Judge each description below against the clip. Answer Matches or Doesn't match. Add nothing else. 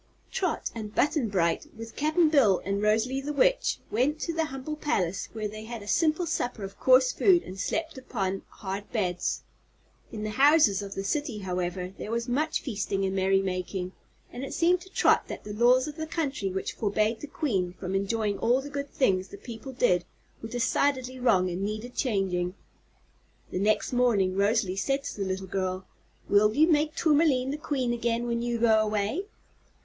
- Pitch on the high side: Matches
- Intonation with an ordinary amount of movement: Doesn't match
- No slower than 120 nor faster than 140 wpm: Doesn't match